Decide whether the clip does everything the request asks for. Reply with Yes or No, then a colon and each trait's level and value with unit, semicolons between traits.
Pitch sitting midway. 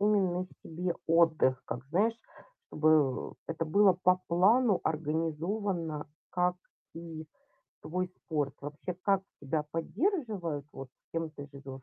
Yes: medium, 165 Hz